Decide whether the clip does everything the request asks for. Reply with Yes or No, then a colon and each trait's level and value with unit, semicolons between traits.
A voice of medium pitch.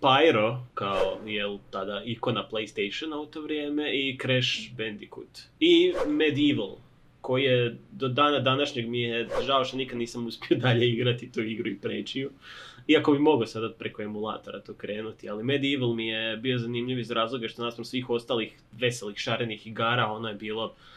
No: low, 120 Hz